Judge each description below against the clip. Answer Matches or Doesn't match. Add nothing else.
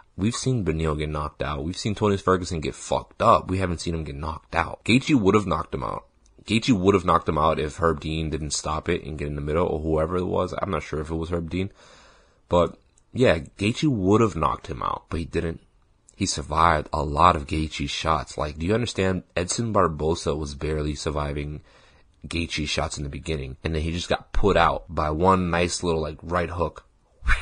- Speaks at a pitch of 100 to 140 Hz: Doesn't match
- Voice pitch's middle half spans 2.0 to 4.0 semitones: Matches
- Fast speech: Matches